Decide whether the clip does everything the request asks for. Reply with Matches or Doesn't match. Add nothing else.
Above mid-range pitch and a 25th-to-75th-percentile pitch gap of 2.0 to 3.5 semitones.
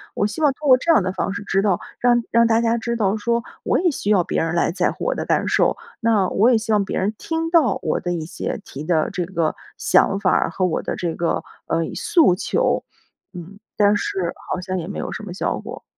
Doesn't match